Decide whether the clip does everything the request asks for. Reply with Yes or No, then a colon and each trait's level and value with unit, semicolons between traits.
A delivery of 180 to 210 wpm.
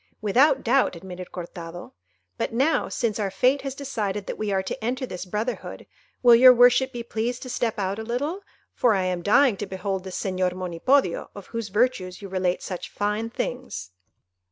Yes: average, 185 wpm